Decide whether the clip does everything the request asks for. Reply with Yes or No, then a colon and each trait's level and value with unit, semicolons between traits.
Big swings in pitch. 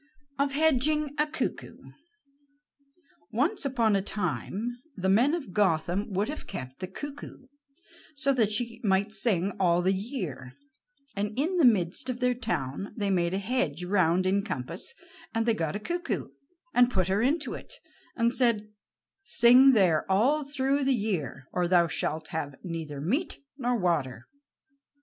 Yes: wide, 6.4 semitones